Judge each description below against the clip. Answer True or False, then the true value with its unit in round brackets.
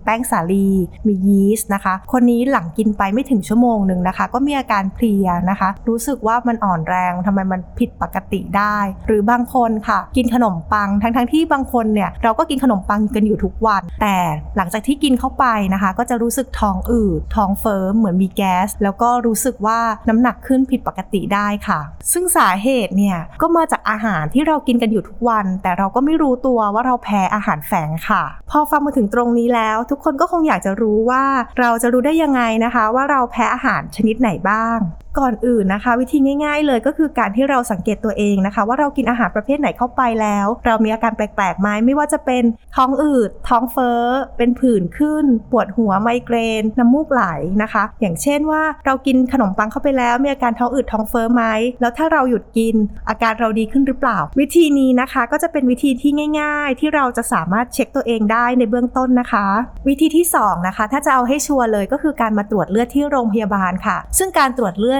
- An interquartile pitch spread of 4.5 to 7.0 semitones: False (4.0 semitones)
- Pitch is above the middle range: True (235 Hz)